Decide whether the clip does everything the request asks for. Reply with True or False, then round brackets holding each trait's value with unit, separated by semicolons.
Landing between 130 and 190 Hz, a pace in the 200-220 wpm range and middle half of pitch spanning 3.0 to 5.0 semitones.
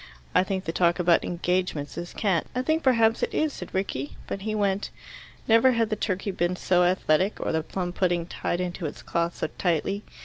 True (185 Hz; 205 wpm; 3.4 semitones)